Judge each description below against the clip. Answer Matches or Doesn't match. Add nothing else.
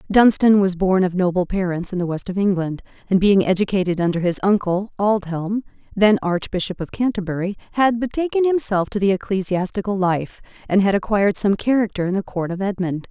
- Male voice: Doesn't match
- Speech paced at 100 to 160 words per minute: Doesn't match